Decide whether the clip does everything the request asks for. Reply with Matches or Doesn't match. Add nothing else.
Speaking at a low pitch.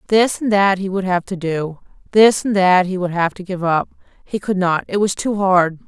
Doesn't match